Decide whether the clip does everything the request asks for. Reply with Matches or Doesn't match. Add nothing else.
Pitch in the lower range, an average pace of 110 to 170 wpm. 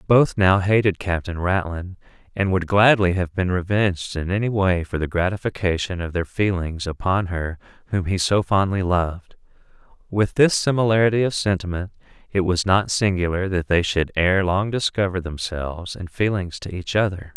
Matches